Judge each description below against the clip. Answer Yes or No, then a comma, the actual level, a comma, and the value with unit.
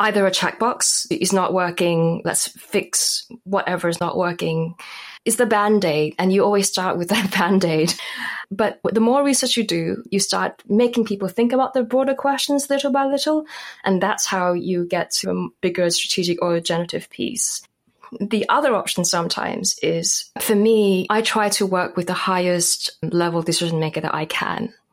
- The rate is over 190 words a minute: No, average, 180 wpm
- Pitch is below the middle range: No, high, 190 Hz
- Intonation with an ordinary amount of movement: Yes, average, 4.4 semitones